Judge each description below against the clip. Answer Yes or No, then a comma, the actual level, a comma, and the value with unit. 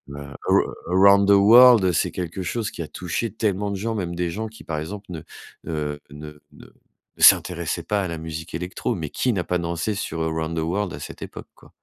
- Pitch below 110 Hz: Yes, very low, 90 Hz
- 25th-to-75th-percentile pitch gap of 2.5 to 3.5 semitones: No, average, 3.9 semitones